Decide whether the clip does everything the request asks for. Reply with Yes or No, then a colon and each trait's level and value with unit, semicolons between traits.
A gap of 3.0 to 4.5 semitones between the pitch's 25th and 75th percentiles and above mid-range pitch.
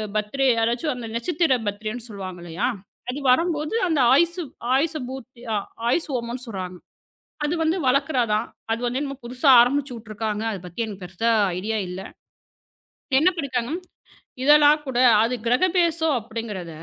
No: average, 5.1 semitones; high, 245 Hz